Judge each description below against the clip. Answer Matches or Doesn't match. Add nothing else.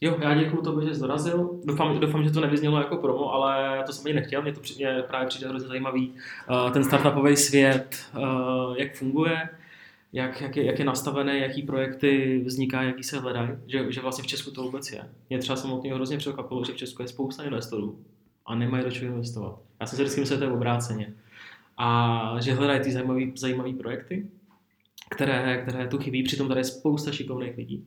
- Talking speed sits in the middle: Doesn't match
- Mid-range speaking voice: Doesn't match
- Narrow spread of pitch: Matches